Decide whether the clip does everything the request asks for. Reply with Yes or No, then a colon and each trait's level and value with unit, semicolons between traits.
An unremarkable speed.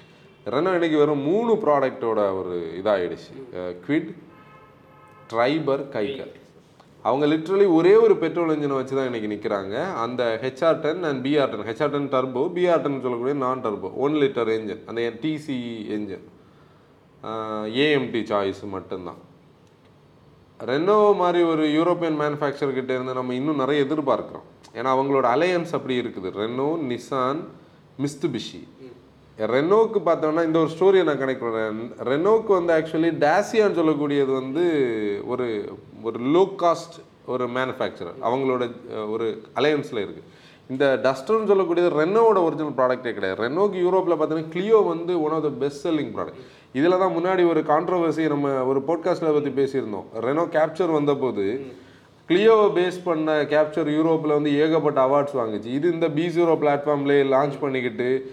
No: fast, 135 wpm